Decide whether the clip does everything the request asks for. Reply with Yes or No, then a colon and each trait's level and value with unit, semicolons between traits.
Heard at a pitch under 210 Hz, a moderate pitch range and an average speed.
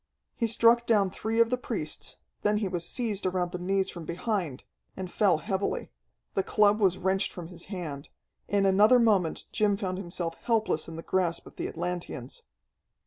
Yes: high, 190 Hz; average, 3.3 semitones; average, 180 wpm